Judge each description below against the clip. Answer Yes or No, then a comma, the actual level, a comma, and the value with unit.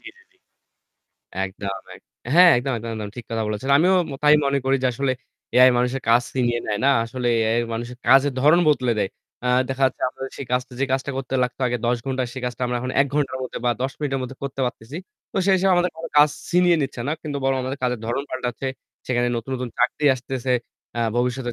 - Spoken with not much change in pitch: Yes, narrow, 2.3 semitones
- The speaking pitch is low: Yes, low, 130 Hz